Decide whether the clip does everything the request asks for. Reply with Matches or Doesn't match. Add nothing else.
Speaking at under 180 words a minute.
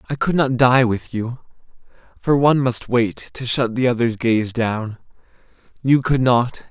Matches